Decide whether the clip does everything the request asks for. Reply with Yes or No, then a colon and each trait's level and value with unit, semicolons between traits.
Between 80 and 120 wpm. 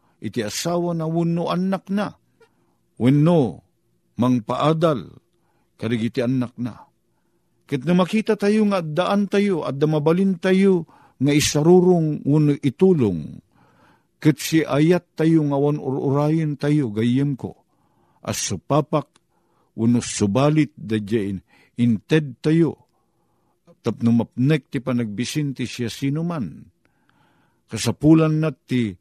Yes: slow, 110 wpm